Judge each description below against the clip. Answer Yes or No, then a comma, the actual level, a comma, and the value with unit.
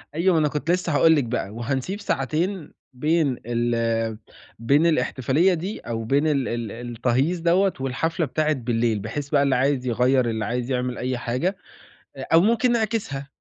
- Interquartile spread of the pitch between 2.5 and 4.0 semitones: No, wide, 5.4 semitones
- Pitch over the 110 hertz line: Yes, low, 135 Hz